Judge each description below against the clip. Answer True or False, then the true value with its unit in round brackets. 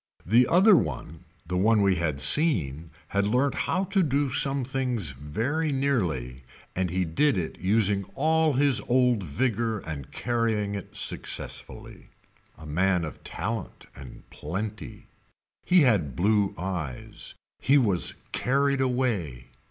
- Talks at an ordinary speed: False (130 wpm)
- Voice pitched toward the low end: True (105 Hz)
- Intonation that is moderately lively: False (7.8 semitones)